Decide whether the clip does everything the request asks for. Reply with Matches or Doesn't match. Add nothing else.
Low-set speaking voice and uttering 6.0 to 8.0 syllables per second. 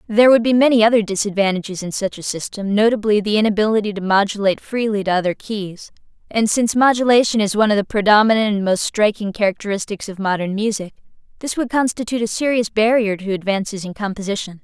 Doesn't match